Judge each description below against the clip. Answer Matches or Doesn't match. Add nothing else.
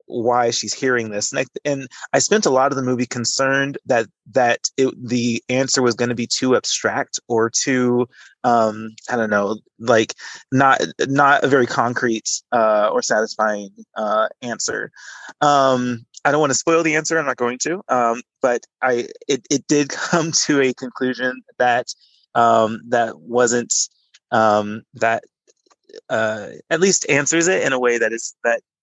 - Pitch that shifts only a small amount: Doesn't match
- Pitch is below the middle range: Matches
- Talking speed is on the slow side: Doesn't match